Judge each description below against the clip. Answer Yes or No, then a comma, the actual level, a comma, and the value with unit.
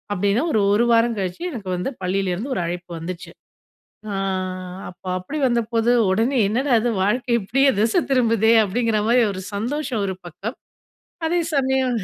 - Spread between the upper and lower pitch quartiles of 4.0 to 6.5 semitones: Yes, average, 4.7 semitones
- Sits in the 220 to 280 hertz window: Yes, high, 225 Hz